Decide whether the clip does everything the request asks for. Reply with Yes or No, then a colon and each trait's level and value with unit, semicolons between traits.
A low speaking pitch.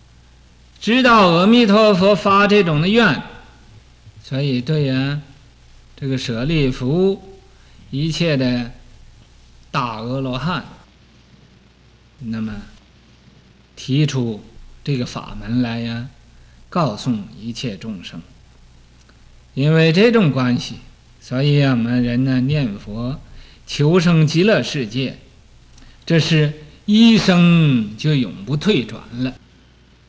Yes: low, 130 Hz